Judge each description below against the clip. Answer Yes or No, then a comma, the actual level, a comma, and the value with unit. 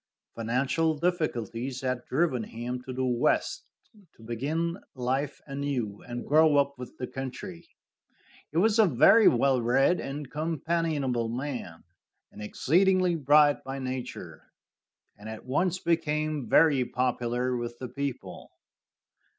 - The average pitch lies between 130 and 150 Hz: Yes, low, 135 Hz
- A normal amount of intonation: Yes, average, 4.1 semitones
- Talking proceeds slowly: Yes, slow, 125 wpm